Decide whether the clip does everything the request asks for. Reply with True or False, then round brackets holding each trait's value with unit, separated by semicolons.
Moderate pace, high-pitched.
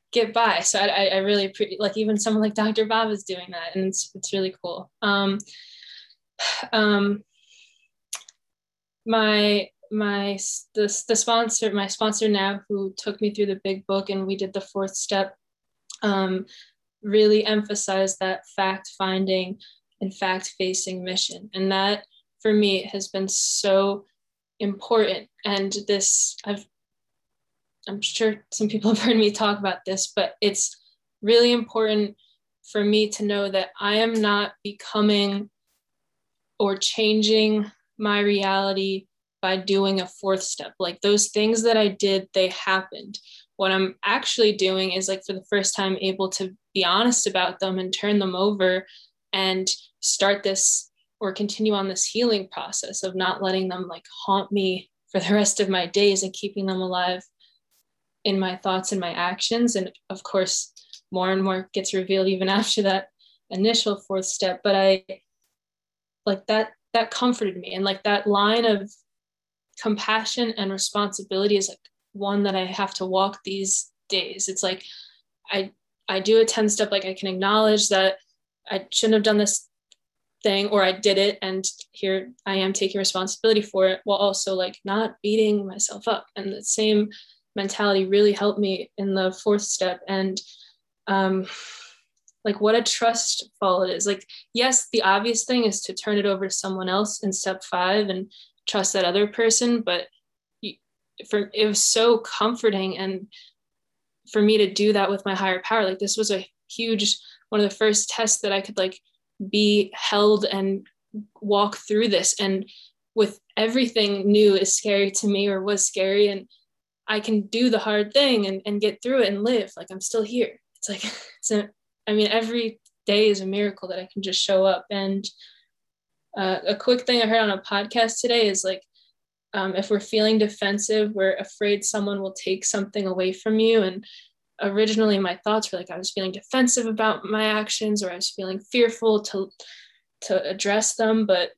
True (170 wpm; 200 Hz)